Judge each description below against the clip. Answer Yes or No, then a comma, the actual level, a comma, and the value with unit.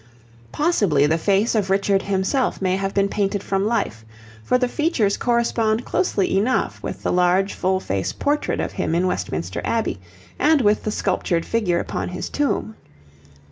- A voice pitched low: No, high, 200 Hz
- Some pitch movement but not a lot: Yes, average, 3.9 semitones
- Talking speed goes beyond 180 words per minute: No, average, 165 wpm